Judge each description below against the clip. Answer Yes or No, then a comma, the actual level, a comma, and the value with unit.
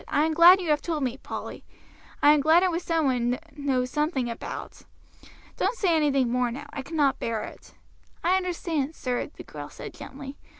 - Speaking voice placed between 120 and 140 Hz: No, very high, 290 Hz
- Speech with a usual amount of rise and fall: Yes, average, 3.9 semitones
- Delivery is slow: No, average, 200 wpm